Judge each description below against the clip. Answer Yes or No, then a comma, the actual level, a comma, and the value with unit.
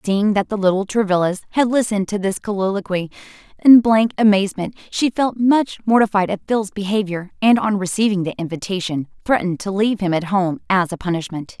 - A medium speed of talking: Yes, average, 175 wpm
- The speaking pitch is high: Yes, high, 200 Hz